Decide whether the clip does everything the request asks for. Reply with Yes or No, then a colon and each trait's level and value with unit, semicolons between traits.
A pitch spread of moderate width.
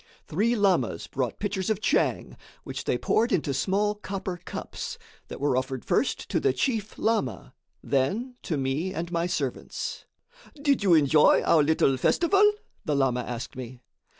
No: wide, 7.7 semitones